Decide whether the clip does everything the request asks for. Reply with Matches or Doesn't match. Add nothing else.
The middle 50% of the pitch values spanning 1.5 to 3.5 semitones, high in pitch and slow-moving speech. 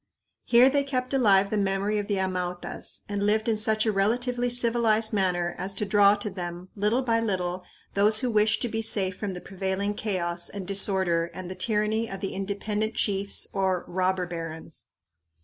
Doesn't match